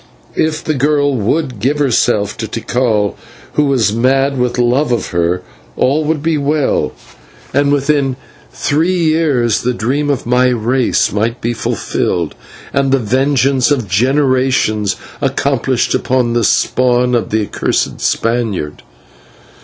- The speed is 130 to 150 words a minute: Yes, slow, 135 wpm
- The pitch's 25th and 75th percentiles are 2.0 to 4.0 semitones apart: Yes, average, 3.7 semitones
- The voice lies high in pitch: No, low, 125 Hz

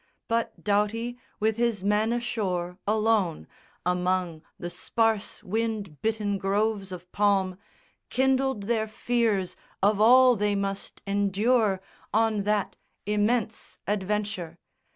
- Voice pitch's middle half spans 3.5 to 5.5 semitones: No, narrow, 2.5 semitones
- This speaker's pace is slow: Yes, slow, 110 wpm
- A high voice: Yes, high, 210 Hz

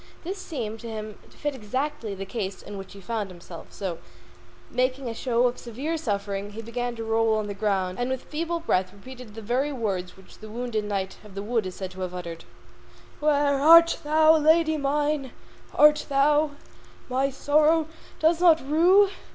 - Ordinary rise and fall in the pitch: No, wide, 6.6 semitones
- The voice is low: No, high, 245 Hz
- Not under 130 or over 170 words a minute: No, average, 185 wpm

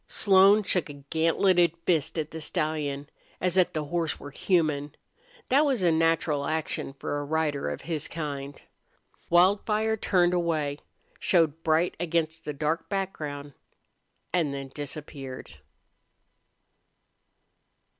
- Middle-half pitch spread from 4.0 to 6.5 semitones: No, average, 3.4 semitones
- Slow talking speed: Yes, slow, 125 wpm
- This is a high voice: No, medium, 160 Hz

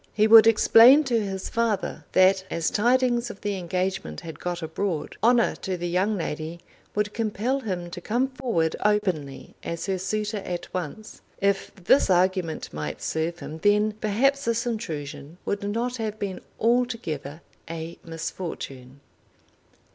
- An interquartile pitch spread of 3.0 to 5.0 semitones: Yes, average, 4.7 semitones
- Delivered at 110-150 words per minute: Yes, average, 145 wpm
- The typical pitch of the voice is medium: No, high, 195 Hz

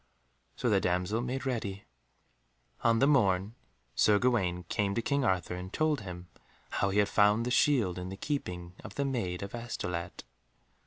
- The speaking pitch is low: Yes, low, 105 Hz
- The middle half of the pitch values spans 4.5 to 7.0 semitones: Yes, average, 5.1 semitones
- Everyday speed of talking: Yes, average, 170 wpm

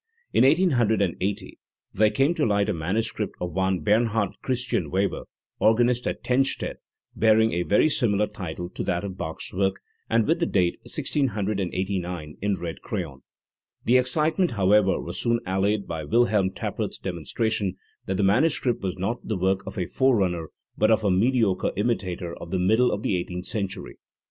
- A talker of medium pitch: No, low, 100 Hz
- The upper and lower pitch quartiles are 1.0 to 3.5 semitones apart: No, average, 4.0 semitones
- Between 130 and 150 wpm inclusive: No, average, 165 wpm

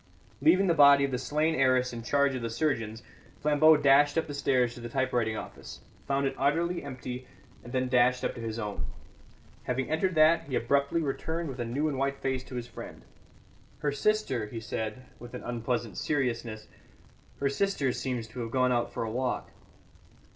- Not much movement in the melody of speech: No, average, 3.3 semitones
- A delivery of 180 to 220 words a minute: Yes, average, 190 wpm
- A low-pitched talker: Yes, low, 130 Hz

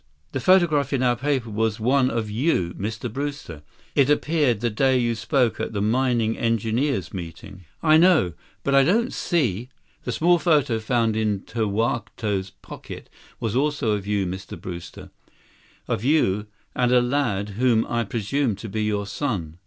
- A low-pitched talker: Yes, low, 115 Hz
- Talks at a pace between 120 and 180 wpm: Yes, average, 160 wpm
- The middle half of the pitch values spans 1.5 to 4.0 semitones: No, average, 4.9 semitones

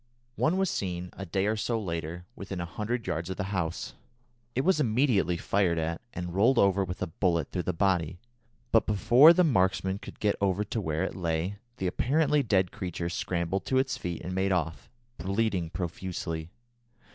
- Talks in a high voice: No, very low, 95 Hz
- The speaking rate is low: No, average, 185 wpm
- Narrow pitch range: No, average, 3.7 semitones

